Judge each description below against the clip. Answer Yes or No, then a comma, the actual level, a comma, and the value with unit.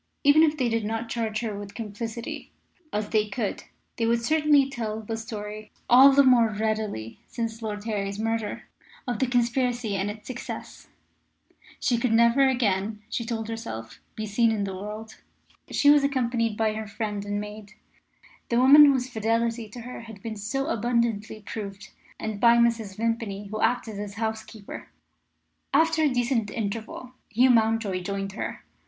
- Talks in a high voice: Yes, high, 225 Hz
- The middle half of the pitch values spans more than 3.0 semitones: No, narrow, 2.4 semitones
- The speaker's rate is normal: Yes, average, 165 wpm